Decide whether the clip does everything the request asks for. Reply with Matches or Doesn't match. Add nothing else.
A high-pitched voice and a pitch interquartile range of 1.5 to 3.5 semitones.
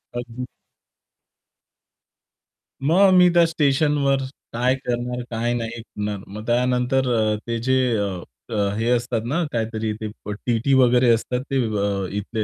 Doesn't match